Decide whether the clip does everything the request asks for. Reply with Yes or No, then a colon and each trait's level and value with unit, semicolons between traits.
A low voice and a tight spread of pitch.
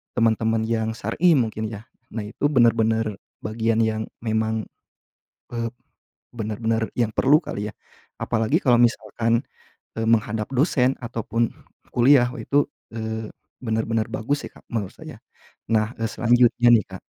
Yes: low, 115 Hz; narrow, 1.4 semitones